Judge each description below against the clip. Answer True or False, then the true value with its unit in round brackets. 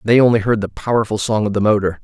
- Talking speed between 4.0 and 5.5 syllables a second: False (6.7 syllables/s)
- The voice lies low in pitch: True (110 Hz)